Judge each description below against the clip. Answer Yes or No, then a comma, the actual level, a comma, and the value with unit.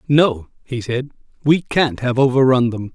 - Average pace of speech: Yes, average, 185 wpm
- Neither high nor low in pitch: No, low, 130 Hz